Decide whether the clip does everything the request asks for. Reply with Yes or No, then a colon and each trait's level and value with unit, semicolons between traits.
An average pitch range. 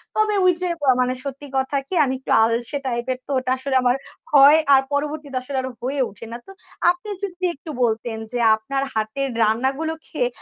Yes: average, 3.2 semitones